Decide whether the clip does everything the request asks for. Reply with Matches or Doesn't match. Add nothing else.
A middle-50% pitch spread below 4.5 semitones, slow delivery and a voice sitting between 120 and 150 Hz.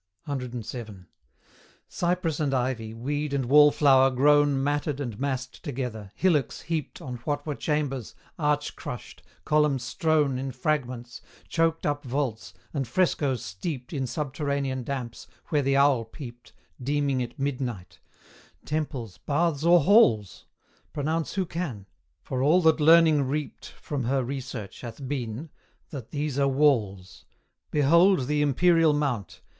Matches